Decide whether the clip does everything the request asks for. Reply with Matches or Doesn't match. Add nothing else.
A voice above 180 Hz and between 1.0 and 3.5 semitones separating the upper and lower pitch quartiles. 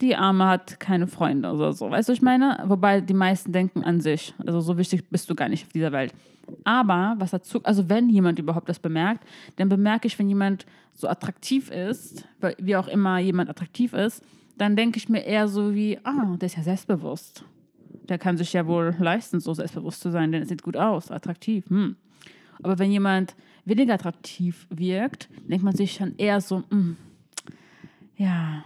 Matches